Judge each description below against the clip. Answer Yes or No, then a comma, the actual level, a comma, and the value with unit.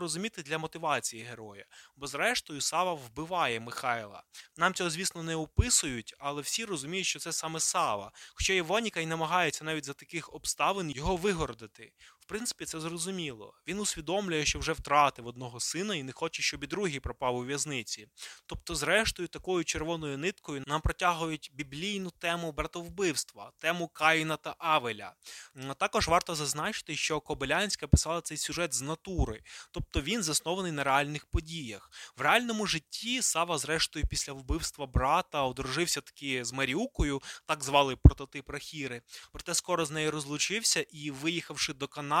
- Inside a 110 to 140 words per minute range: No, average, 150 wpm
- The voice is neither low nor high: Yes, medium, 155 Hz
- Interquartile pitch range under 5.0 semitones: Yes, average, 3.4 semitones